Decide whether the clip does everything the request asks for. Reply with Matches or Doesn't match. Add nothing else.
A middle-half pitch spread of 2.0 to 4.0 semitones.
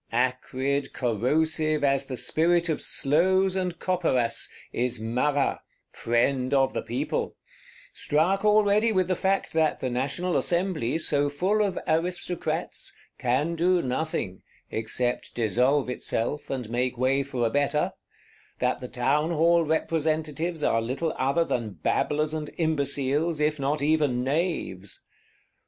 Doesn't match